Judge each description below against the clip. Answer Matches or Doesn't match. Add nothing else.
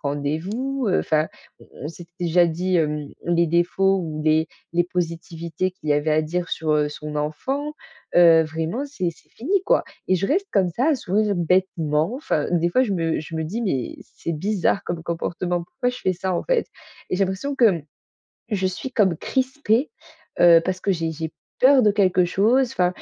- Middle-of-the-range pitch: Matches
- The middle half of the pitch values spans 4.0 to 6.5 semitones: Matches